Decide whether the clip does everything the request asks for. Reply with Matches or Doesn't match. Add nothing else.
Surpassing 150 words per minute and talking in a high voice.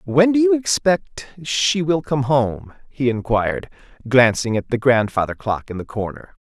Doesn't match